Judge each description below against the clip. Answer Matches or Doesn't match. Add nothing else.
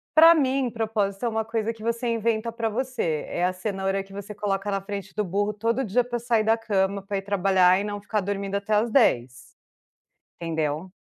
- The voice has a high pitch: Matches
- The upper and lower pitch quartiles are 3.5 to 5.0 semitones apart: Doesn't match